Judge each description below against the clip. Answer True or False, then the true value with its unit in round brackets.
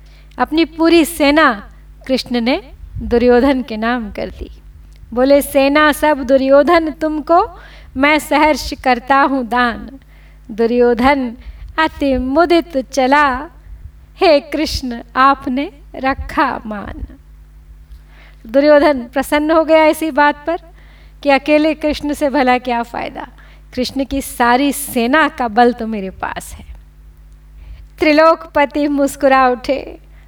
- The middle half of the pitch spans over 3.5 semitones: True (3.9 semitones)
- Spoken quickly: False (110 wpm)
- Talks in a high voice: True (275 Hz)